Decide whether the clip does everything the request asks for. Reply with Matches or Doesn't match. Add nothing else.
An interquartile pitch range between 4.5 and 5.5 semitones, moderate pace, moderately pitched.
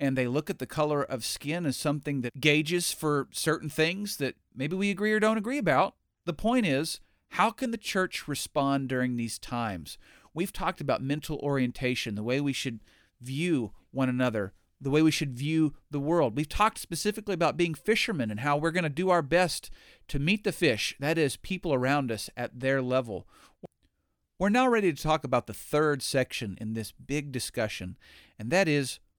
Matches